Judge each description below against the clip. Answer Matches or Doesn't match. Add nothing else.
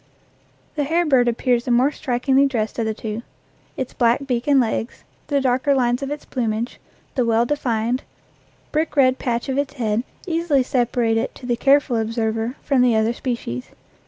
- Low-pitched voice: Doesn't match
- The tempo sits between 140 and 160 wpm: Doesn't match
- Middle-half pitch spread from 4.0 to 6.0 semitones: Doesn't match